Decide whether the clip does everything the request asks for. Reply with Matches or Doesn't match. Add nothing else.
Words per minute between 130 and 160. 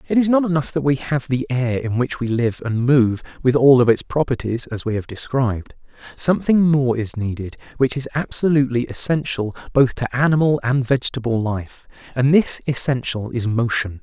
Doesn't match